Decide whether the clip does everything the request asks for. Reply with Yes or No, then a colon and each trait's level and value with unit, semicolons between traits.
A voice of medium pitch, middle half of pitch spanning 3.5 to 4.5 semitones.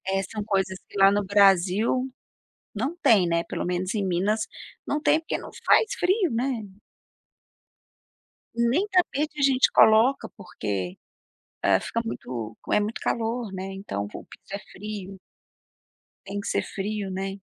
No: high, 205 Hz; average, 4.1 semitones